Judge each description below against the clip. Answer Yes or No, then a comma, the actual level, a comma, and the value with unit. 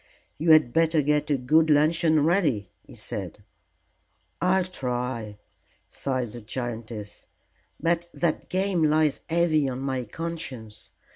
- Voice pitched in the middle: Yes, medium, 150 Hz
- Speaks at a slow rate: Yes, slow, 125 wpm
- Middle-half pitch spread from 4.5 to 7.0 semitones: Yes, average, 5.1 semitones